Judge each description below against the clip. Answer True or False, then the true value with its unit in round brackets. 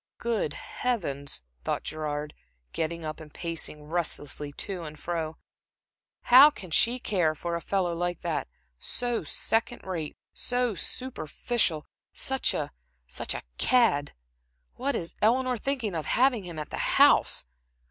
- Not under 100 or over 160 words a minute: True (140 wpm)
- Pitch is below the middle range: False (175 Hz)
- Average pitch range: False (7.4 semitones)